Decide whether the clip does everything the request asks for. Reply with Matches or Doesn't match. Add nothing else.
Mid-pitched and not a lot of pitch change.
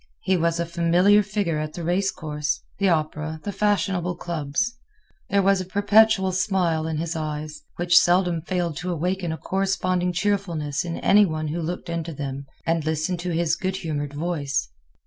Doesn't match